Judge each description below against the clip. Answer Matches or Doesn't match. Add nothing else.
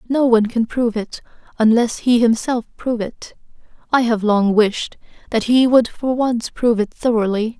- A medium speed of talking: Matches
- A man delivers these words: Doesn't match